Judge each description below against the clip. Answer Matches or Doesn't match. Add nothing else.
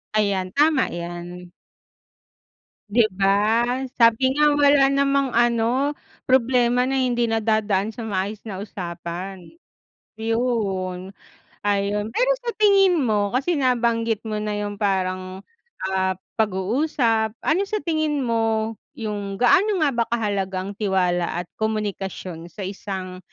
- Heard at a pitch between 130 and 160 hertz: Doesn't match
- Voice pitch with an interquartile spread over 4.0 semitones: Matches